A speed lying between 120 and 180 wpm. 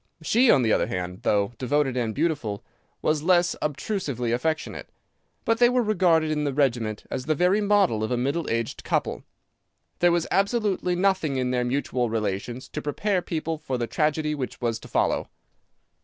Yes: average, 175 wpm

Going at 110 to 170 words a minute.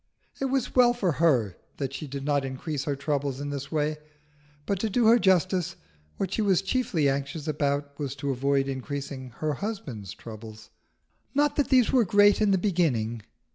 No: average, 180 wpm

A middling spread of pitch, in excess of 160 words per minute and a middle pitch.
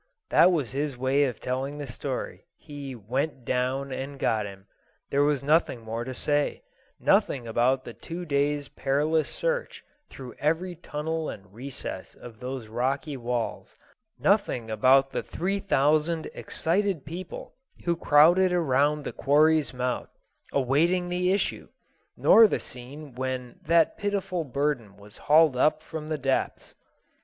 No: average, 4.0 semitones; average, 145 wpm; medium, 145 Hz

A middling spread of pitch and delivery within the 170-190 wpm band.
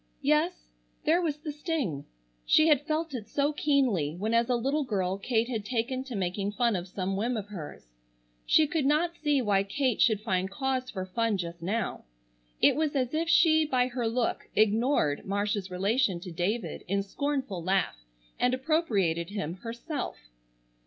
No: wide, 6.6 semitones; average, 175 wpm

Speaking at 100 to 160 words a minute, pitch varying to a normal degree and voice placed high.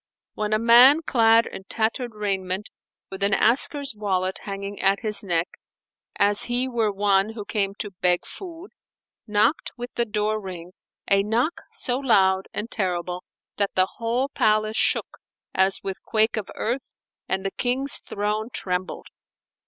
Yes: average, 150 wpm; average, 3.2 semitones; high, 210 Hz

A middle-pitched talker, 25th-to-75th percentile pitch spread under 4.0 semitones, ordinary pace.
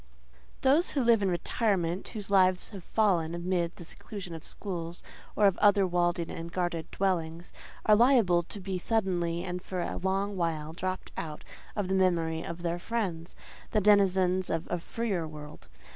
Yes: medium, 180 Hz; average, 2.9 semitones; average, 175 wpm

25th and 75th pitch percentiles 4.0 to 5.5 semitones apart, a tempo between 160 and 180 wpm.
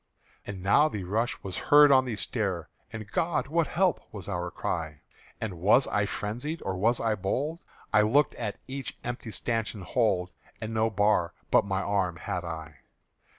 Yes: average, 4.6 semitones; average, 175 wpm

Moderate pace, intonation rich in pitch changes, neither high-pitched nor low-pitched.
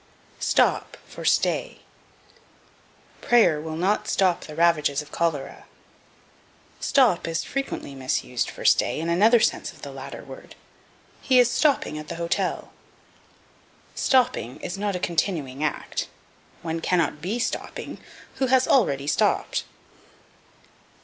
No: slow, 125 wpm; wide, 6.7 semitones; medium, 170 Hz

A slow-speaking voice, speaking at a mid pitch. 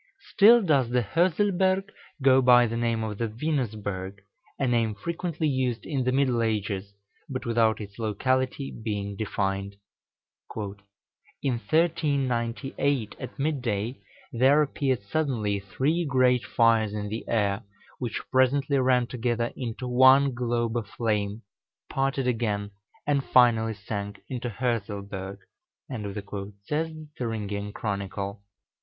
No: slow, 125 wpm; low, 120 Hz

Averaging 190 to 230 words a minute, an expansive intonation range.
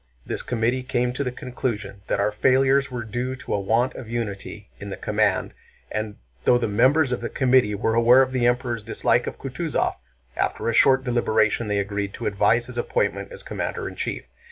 No: average, 200 wpm; average, 3.3 semitones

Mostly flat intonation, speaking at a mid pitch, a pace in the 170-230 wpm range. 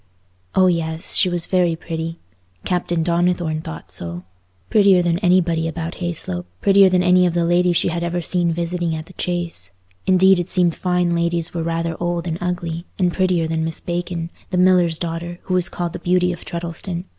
Yes: narrow, 1.5 semitones; medium, 175 Hz; average, 180 wpm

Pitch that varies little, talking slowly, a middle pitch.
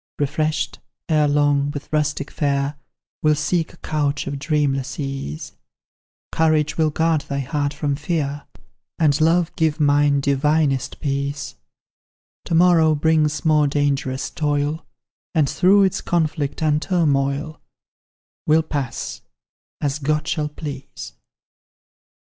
Yes: narrow, 1.8 semitones; slow, 115 wpm; medium, 150 Hz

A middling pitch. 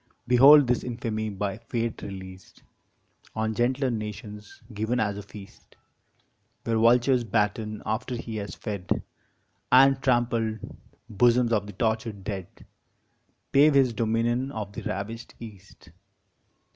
No: low, 110 Hz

